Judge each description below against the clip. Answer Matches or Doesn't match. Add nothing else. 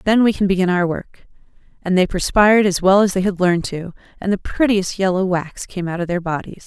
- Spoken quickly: Matches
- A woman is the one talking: Matches